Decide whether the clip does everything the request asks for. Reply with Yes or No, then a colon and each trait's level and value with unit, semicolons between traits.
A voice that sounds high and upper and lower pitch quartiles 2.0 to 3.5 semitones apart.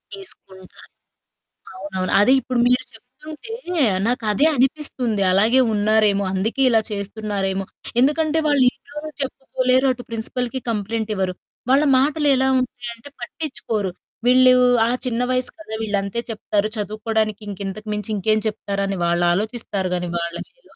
No: high, 225 Hz; average, 4.3 semitones